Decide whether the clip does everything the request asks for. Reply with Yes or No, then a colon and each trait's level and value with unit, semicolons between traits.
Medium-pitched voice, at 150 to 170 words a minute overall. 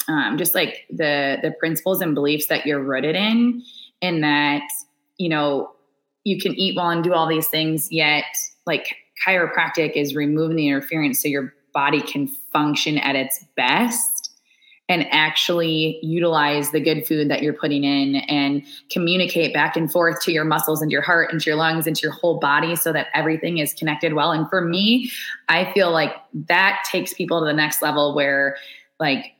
No: medium, 155 Hz; average, 185 wpm